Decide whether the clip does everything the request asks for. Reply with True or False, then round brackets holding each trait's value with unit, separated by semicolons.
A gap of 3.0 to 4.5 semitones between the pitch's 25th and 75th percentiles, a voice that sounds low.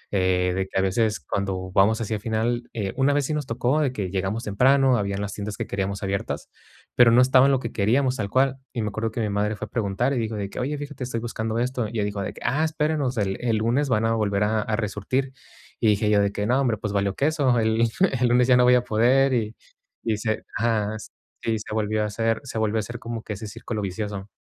True (3.4 semitones; 110 Hz)